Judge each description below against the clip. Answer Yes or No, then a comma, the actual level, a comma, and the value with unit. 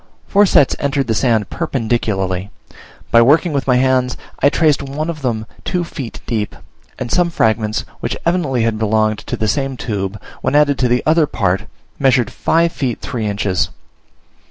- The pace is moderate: Yes, average, 170 wpm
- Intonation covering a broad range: No, average, 4.8 semitones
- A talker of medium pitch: No, low, 125 Hz